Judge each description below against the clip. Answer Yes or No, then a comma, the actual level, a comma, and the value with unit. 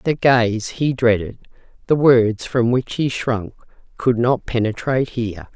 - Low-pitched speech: Yes, low, 120 Hz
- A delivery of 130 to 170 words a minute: Yes, average, 150 wpm